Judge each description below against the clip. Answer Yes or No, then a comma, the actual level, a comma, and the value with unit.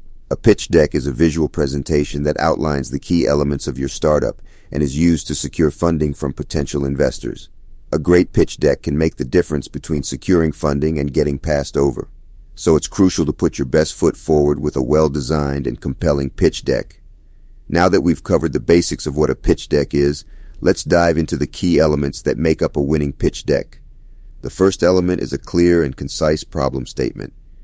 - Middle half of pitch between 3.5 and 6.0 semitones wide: No, narrow, 2.4 semitones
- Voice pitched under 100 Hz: Yes, very low, 75 Hz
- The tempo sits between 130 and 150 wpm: No, average, 195 wpm